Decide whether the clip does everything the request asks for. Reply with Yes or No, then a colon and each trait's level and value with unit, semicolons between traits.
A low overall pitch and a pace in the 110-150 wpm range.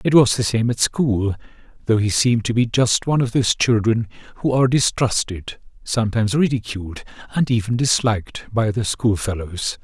No: low, 115 Hz; average, 165 wpm